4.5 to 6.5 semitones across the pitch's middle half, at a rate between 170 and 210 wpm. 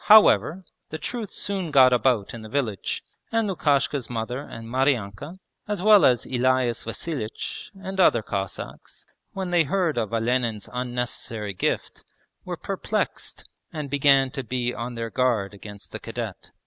No: wide, 5.4 semitones; average, 150 wpm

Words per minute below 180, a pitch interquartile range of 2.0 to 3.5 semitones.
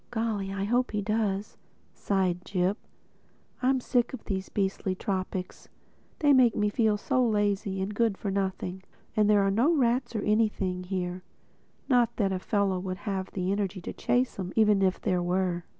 Yes: average, 165 wpm; average, 2.9 semitones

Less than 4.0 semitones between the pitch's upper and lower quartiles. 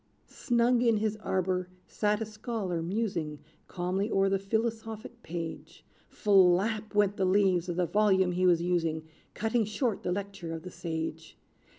Yes: average, 3.5 semitones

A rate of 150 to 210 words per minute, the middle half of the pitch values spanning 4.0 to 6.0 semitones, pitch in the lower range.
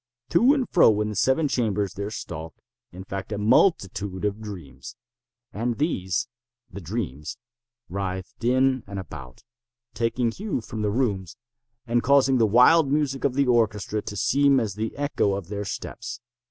Yes: average, 155 wpm; average, 4.4 semitones; low, 110 Hz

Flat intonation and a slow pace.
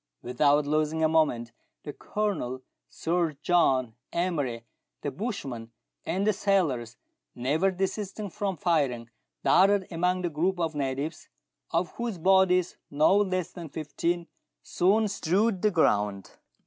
No: average, 5.0 semitones; slow, 125 wpm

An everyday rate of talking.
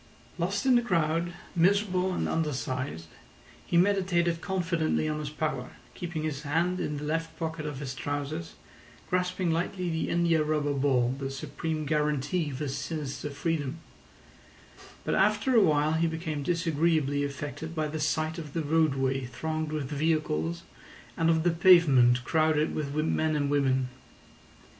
Yes: average, 150 wpm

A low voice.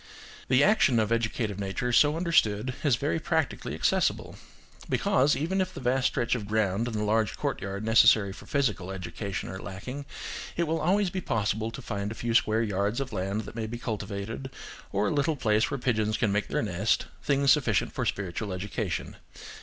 Yes: low, 110 Hz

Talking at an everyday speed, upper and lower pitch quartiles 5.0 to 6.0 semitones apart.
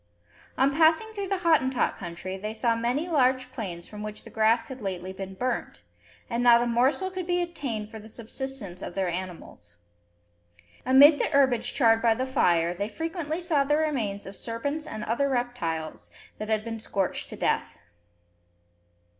Yes: average, 170 wpm; wide, 5.4 semitones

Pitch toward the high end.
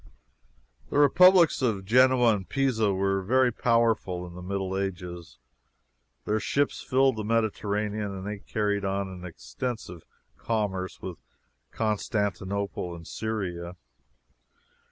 No: low, 100 Hz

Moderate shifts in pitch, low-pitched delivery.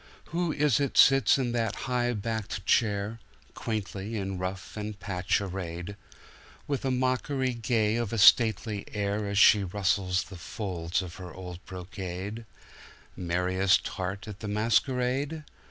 Yes: average, 4.1 semitones; low, 105 Hz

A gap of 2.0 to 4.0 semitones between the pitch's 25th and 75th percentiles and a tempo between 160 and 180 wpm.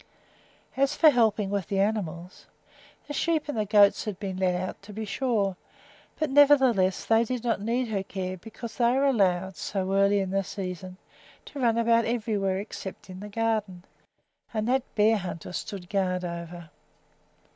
Yes: average, 3.7 semitones; average, 165 wpm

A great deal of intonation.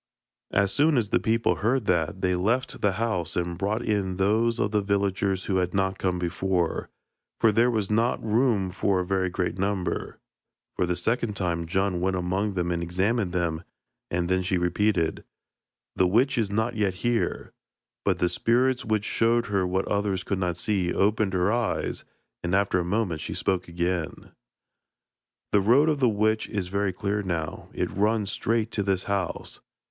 No: average, 3.2 semitones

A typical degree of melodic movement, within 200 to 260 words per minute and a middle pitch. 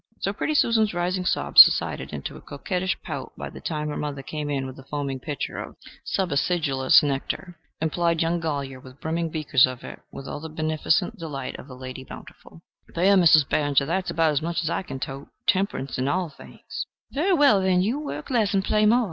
Yes: average, 4.9 semitones; fast, 205 wpm; medium, 160 Hz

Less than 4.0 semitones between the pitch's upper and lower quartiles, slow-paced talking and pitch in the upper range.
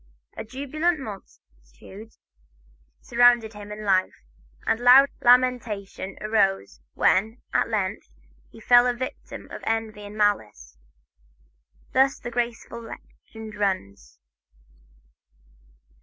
Yes: average, 3.6 semitones; slow, 100 wpm; high, 220 Hz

